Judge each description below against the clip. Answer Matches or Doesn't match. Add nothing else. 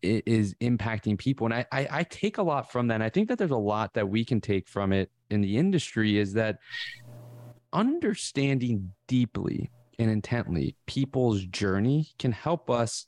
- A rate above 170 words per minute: Matches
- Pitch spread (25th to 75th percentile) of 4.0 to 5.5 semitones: Matches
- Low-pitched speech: Matches